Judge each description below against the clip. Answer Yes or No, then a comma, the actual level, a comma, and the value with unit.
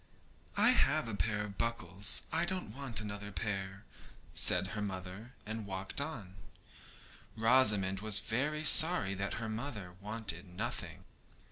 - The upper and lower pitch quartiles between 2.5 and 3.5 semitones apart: Yes, average, 3.2 semitones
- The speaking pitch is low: Yes, low, 105 Hz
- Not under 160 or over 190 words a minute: No, slow, 135 wpm